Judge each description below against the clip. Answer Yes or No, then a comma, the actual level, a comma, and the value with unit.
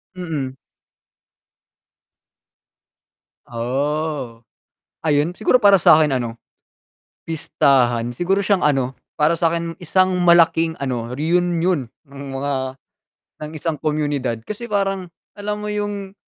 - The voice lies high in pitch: No, medium, 155 Hz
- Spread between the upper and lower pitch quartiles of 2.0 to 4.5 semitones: No, average, 5.2 semitones